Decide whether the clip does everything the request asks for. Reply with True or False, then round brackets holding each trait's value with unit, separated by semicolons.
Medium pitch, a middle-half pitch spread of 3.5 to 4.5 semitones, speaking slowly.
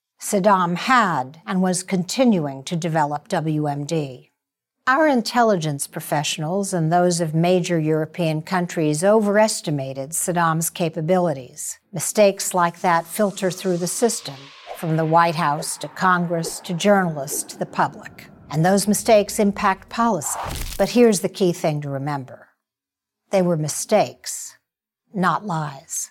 True (175 Hz; 3.9 semitones; 125 wpm)